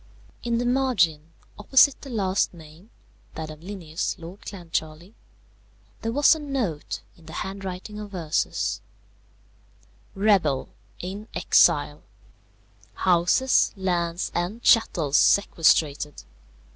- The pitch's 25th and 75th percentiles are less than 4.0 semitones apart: No, average, 4.8 semitones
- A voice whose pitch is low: No, medium, 185 Hz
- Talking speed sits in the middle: No, slow, 105 wpm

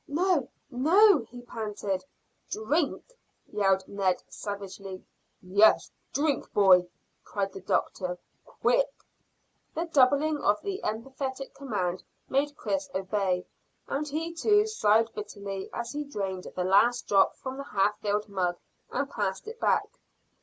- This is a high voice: Yes, high, 220 Hz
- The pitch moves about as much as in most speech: No, wide, 6.9 semitones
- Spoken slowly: Yes, slow, 130 wpm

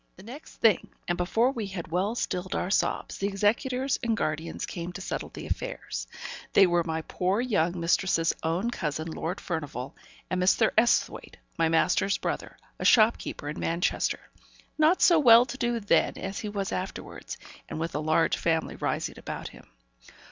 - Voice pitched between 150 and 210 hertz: Yes, high, 190 Hz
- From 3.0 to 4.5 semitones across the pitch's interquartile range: No, wide, 5.5 semitones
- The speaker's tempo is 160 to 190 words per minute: Yes, average, 170 wpm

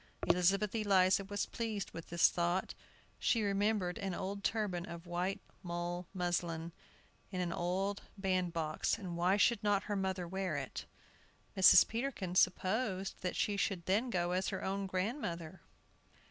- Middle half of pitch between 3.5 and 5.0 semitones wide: No, narrow, 2.5 semitones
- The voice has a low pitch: No, medium, 185 Hz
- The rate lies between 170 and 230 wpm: No, average, 145 wpm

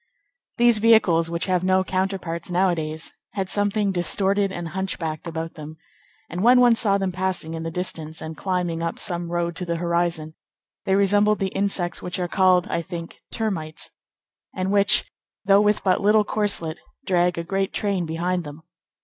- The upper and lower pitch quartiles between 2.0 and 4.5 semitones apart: Yes, average, 2.8 semitones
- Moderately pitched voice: Yes, medium, 180 Hz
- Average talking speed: Yes, average, 170 wpm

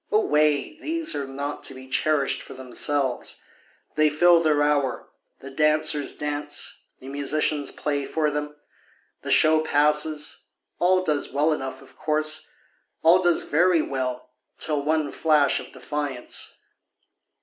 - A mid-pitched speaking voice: Yes, medium, 150 Hz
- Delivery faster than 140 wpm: No, slow, 135 wpm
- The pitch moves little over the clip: Yes, narrow, 1.7 semitones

